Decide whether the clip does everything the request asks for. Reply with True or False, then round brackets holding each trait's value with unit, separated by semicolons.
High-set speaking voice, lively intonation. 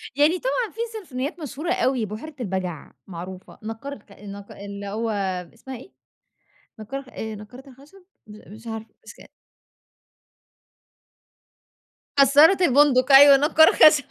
True (260 Hz; 5.7 semitones)